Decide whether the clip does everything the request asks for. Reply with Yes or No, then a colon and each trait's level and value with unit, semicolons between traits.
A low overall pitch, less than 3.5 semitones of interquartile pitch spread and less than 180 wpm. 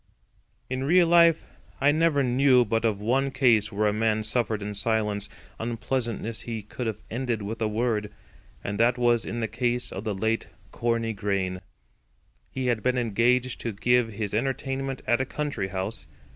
Yes: low, 115 Hz; average, 3.0 semitones; average, 170 wpm